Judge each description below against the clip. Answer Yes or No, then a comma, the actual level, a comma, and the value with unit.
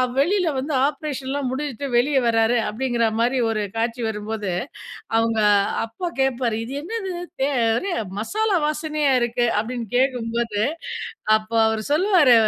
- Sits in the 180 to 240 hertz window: No, very high, 250 Hz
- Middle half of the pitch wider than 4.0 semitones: Yes, average, 4.5 semitones